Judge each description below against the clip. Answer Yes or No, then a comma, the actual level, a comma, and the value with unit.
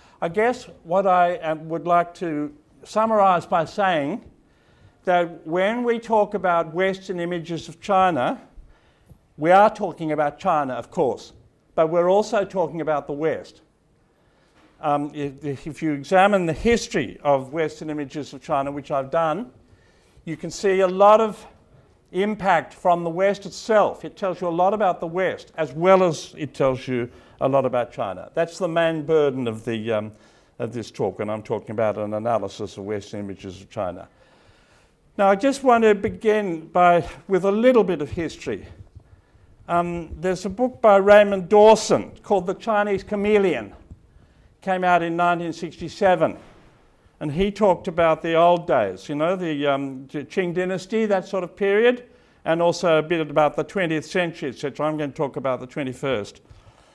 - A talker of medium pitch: Yes, medium, 170 Hz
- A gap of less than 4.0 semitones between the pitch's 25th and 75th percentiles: No, average, 4.8 semitones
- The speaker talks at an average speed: Yes, average, 170 wpm